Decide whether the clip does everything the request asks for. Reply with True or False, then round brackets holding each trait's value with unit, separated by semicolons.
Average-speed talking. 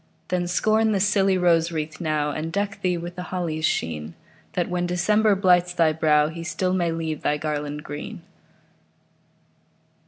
True (160 wpm)